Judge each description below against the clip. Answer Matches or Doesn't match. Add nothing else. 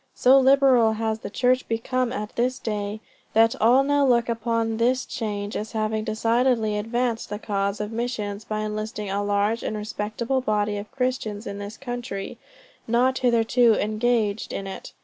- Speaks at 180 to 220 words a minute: Doesn't match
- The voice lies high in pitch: Matches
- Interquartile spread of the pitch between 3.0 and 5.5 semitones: Doesn't match